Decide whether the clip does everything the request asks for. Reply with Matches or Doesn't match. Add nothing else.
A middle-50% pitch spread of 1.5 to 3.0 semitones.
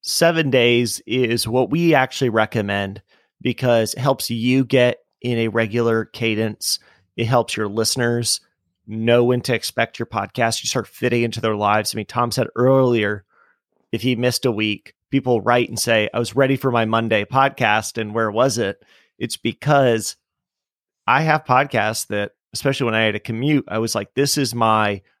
Matches